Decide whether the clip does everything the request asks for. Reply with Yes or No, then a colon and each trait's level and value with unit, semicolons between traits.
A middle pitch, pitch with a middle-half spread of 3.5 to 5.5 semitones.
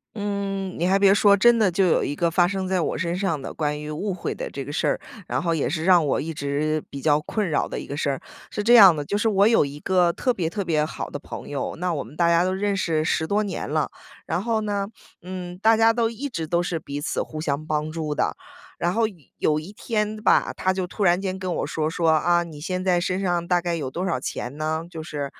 Yes: medium, 175 Hz; average, 4.1 semitones